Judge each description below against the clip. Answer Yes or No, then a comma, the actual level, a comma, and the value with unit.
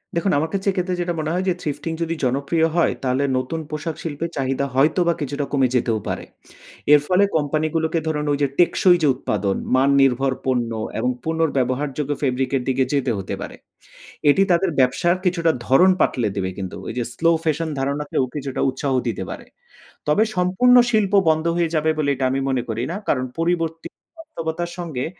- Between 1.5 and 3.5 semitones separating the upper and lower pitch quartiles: No, average, 4.2 semitones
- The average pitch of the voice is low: No, medium, 150 Hz